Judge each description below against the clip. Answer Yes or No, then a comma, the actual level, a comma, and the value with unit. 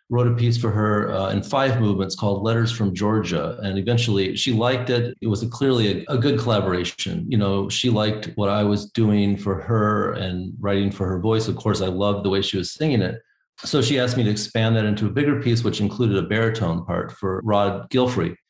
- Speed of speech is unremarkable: No, fast, 225 wpm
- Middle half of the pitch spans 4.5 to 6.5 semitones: No, average, 3.0 semitones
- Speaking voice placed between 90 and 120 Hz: Yes, low, 105 Hz